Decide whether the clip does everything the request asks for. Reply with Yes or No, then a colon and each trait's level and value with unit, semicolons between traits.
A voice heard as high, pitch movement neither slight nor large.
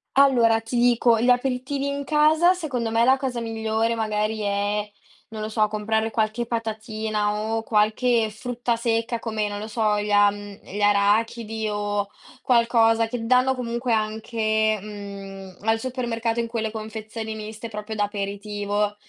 No: high, 220 Hz; narrow, 2.0 semitones